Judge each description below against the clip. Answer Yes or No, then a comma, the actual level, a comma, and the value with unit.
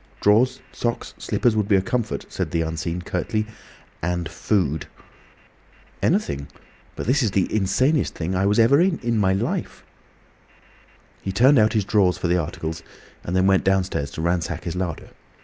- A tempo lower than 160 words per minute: No, average, 165 wpm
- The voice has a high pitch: No, very low, 95 Hz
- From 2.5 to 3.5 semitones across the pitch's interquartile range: No, average, 4.4 semitones